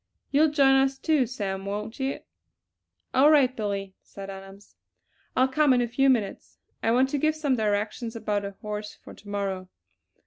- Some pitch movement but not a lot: Yes, average, 4.8 semitones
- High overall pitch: Yes, high, 230 Hz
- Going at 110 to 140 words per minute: No, average, 175 wpm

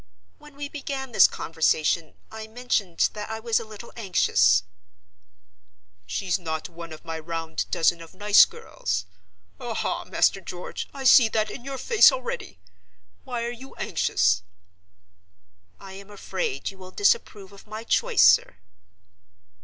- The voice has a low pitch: No, high, 205 Hz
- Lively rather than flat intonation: Yes, wide, 6.7 semitones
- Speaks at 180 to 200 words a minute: No, average, 140 wpm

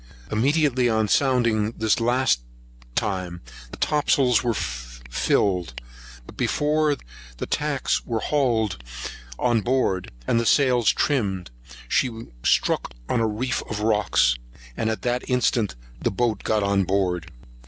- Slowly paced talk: Yes, slow, 130 wpm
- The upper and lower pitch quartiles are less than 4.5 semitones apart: No, average, 4.8 semitones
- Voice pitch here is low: Yes, low, 110 Hz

